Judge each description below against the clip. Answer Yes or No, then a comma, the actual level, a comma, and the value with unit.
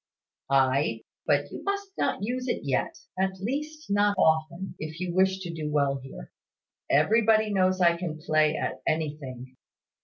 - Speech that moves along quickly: No, average, 155 wpm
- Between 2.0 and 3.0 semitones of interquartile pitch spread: No, wide, 5.4 semitones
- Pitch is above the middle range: No, medium, 170 Hz